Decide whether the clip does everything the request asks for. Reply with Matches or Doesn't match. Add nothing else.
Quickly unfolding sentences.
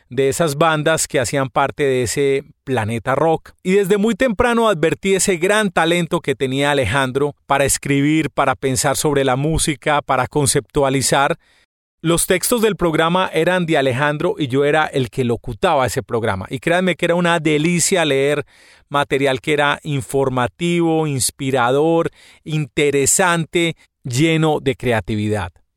Doesn't match